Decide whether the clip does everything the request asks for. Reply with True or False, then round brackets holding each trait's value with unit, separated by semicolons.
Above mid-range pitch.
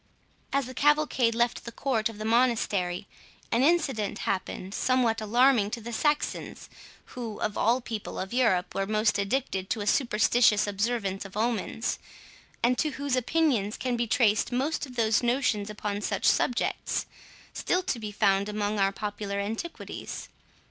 True (225 Hz)